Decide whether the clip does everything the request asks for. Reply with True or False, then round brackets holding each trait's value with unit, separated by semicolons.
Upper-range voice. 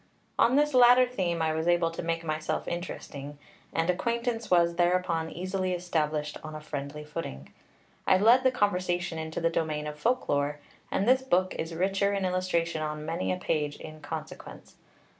False (170 Hz)